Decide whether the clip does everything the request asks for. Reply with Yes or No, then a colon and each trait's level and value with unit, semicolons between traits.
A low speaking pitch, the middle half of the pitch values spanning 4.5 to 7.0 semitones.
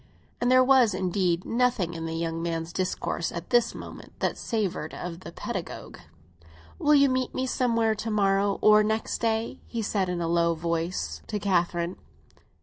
No: high, 195 Hz; average, 5.1 semitones